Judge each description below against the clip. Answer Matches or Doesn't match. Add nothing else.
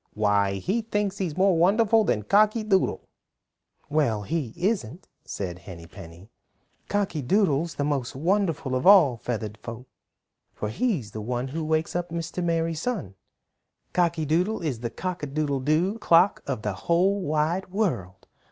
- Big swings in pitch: Matches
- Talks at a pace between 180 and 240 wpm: Doesn't match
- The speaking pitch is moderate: Matches